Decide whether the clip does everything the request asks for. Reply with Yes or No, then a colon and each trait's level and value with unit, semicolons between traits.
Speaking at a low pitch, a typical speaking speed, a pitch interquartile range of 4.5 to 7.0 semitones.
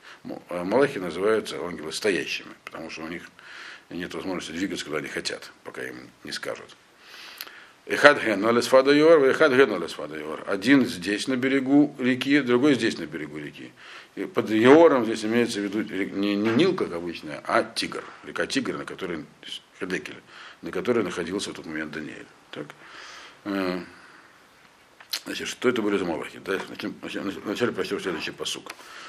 Yes: low, 115 Hz; average, 130 wpm; wide, 5.6 semitones